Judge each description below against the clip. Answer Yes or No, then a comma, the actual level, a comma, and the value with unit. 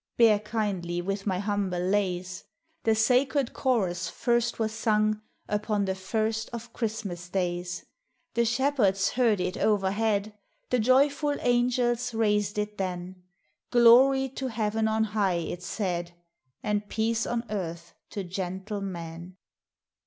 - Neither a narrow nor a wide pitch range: Yes, average, 3.7 semitones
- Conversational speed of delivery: No, slow, 130 wpm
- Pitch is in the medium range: No, high, 210 Hz